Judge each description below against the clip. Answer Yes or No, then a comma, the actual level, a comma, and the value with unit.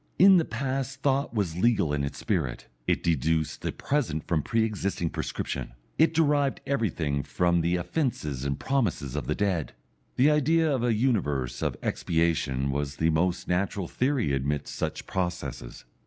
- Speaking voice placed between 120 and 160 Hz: No, very low, 90 Hz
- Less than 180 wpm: Yes, average, 160 wpm